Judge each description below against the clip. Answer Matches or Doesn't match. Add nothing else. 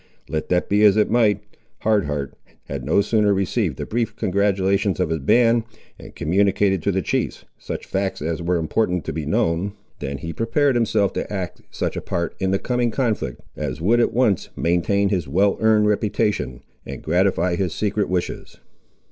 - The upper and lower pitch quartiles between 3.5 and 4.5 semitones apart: Matches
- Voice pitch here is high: Doesn't match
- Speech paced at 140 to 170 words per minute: Doesn't match